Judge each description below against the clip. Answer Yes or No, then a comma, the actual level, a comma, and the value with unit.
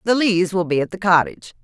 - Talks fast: Yes, fast, 255 wpm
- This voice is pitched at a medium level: Yes, medium, 180 Hz